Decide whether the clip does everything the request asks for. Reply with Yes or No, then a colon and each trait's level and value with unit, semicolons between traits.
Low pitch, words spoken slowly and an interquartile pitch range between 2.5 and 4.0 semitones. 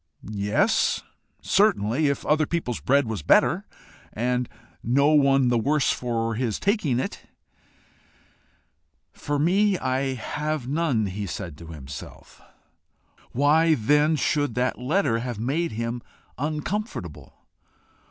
No: low, 130 Hz; slow, 115 wpm; average, 5.1 semitones